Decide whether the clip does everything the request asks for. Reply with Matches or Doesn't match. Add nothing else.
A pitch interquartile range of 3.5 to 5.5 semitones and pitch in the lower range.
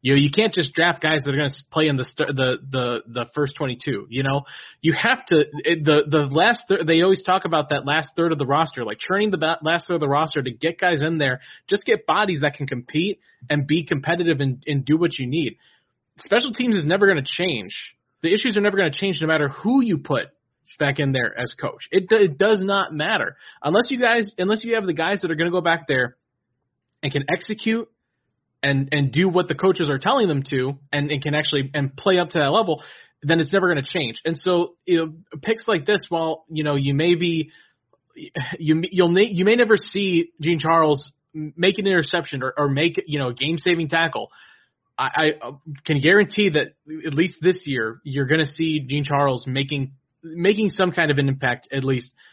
Doesn't match